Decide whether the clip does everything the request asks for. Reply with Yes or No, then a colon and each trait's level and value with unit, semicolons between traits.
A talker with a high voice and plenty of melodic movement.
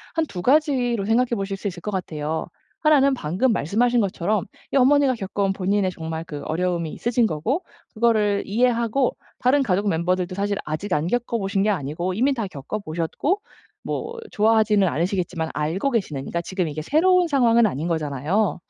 Yes: high, 200 Hz; wide, 6.0 semitones